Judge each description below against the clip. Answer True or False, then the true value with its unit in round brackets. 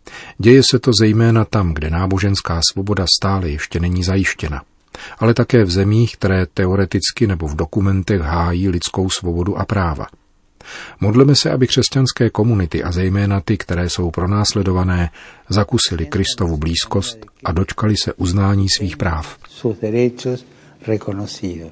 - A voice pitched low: True (100 Hz)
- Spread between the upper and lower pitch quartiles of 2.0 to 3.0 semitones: False (3.8 semitones)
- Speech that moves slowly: False (125 wpm)